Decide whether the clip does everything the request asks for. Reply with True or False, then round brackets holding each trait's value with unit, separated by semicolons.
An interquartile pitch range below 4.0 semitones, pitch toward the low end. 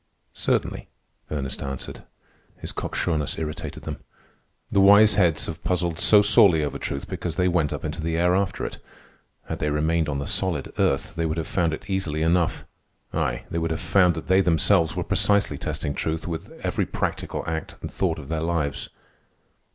True (2.8 semitones; 80 Hz)